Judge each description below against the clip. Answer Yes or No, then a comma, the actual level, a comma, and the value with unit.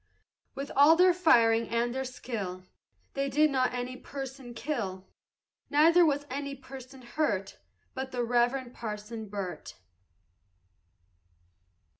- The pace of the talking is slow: Yes, slow, 115 wpm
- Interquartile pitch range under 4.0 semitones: Yes, average, 3.3 semitones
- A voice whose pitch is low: No, very high, 255 Hz